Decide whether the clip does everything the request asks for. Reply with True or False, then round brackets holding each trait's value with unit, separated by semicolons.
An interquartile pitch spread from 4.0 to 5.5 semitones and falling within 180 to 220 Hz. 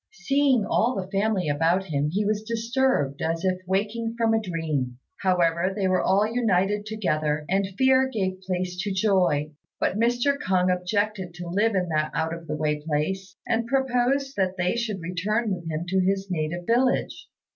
True (4.6 semitones; 190 Hz)